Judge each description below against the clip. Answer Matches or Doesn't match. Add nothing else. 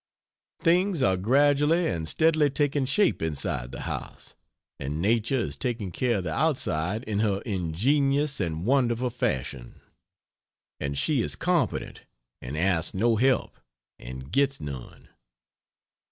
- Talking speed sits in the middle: Doesn't match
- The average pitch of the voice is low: Matches